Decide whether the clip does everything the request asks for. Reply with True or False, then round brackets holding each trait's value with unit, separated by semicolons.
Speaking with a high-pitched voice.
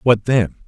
False (115 Hz)